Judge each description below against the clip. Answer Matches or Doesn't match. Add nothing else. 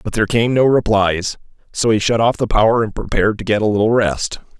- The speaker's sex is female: Doesn't match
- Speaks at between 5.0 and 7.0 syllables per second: Matches